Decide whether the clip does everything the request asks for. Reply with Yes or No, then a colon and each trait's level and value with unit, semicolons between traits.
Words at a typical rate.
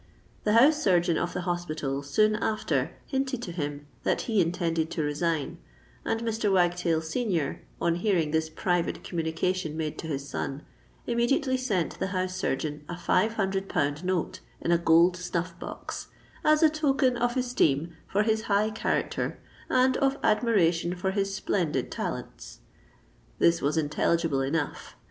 Yes: average, 155 wpm